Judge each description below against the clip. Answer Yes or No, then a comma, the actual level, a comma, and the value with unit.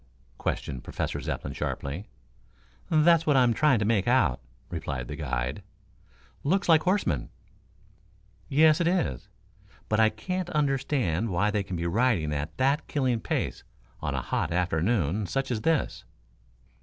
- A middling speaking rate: Yes, average, 145 wpm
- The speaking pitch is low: Yes, low, 110 Hz